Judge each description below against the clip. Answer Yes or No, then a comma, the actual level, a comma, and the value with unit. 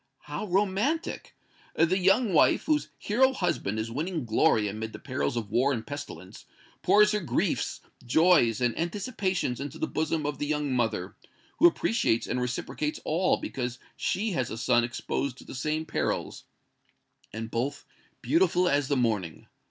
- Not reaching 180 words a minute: Yes, average, 160 wpm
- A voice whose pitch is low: No, medium, 145 Hz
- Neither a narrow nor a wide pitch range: No, wide, 7.7 semitones